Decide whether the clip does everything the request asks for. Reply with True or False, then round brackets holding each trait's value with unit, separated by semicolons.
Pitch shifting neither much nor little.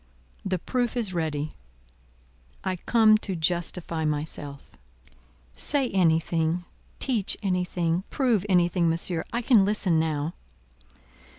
True (4.2 semitones)